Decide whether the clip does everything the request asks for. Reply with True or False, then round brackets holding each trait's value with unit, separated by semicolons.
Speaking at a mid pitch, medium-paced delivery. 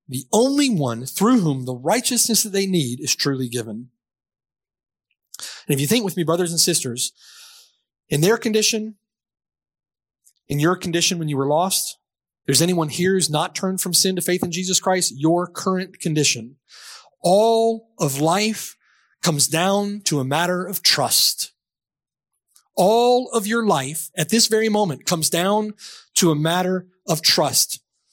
True (180 Hz; 155 wpm)